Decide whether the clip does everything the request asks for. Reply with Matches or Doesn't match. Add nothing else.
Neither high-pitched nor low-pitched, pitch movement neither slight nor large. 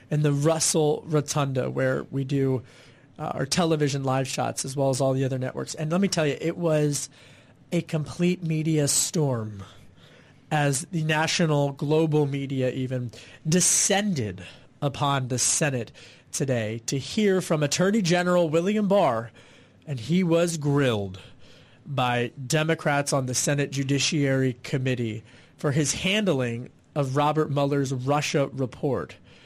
Matches